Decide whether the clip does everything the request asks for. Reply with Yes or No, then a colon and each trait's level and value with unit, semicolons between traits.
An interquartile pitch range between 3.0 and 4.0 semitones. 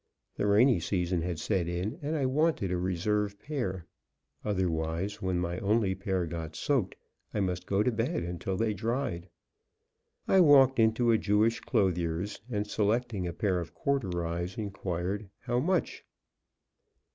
No: average, 4.5 semitones